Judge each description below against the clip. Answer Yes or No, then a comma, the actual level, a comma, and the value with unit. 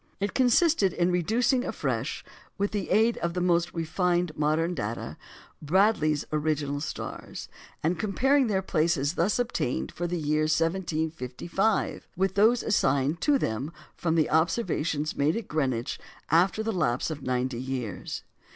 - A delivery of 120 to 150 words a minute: Yes, average, 140 wpm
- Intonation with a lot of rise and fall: No, average, 4.7 semitones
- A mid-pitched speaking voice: Yes, medium, 170 Hz